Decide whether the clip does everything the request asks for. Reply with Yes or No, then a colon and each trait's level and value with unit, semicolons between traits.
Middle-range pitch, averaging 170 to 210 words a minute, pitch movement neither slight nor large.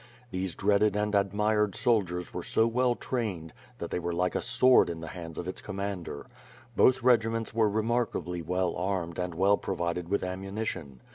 No: low, 100 Hz; average, 180 wpm; average, 3.7 semitones